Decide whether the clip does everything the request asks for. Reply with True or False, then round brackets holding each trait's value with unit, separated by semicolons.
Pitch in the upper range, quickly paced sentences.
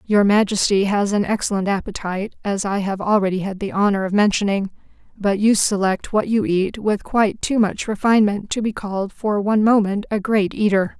False (205 Hz; 190 wpm)